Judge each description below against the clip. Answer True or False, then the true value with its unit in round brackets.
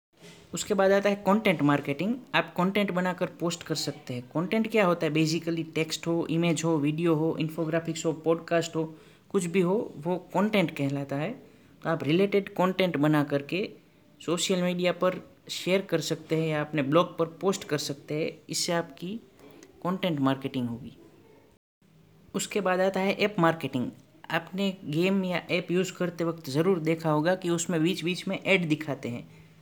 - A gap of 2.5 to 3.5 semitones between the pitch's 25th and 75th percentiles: True (2.9 semitones)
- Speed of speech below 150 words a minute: False (170 wpm)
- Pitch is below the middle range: False (170 Hz)